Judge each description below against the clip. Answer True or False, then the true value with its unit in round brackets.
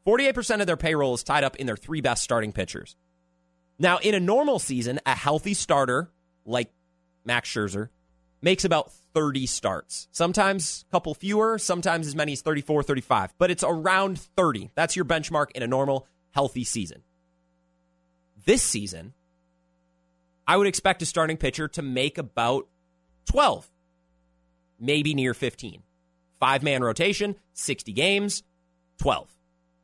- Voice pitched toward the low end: True (130 Hz)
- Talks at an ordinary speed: True (145 wpm)